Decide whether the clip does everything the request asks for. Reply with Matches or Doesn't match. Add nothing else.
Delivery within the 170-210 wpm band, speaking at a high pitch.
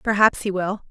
Matches